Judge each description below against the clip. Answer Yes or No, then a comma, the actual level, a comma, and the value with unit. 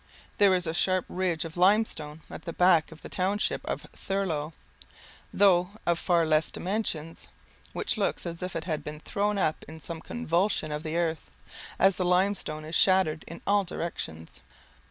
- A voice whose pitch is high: No, medium, 175 Hz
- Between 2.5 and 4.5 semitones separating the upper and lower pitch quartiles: Yes, average, 3.2 semitones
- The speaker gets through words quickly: No, average, 175 wpm